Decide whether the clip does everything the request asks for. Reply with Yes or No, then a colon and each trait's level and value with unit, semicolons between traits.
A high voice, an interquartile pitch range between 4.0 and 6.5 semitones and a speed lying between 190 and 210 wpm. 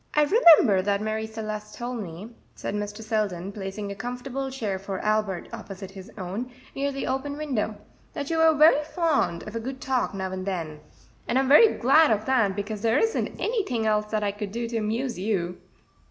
Yes: high, 220 Hz; average, 5.0 semitones; average, 195 wpm